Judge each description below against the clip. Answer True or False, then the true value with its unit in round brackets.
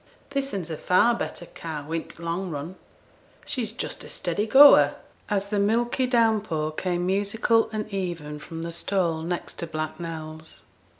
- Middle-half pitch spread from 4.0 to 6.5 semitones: True (4.9 semitones)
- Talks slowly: False (170 wpm)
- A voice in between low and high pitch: True (180 Hz)